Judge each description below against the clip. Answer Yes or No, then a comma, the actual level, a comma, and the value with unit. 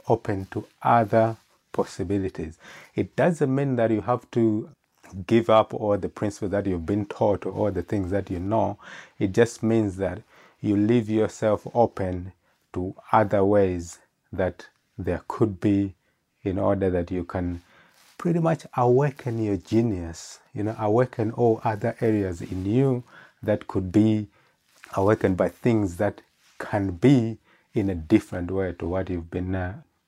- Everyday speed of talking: Yes, average, 155 wpm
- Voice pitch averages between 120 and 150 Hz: No, low, 105 Hz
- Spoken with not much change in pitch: No, average, 3.3 semitones